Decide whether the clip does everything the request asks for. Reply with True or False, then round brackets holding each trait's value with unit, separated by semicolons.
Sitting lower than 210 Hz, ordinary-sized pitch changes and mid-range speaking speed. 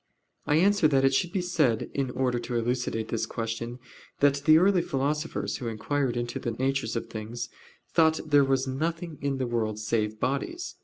True (135 Hz; 4.5 semitones; 185 wpm)